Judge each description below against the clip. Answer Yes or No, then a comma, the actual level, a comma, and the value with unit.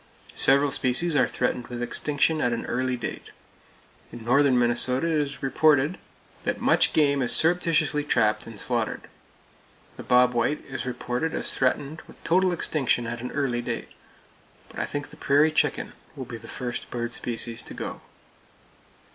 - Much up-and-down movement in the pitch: No, average, 3.5 semitones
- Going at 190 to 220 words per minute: No, average, 165 wpm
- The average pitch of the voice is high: No, low, 130 Hz